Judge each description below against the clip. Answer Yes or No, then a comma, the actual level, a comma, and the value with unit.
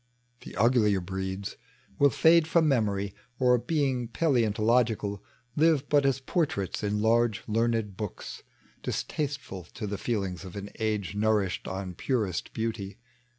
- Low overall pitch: Yes, low, 110 Hz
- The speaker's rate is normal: No, slow, 130 wpm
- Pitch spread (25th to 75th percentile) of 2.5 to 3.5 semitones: No, average, 4.4 semitones